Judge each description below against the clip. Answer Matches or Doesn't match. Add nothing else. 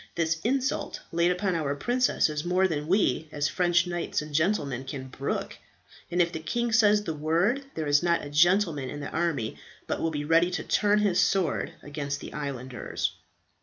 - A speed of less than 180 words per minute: Doesn't match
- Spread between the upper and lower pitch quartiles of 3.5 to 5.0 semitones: Matches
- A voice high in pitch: Doesn't match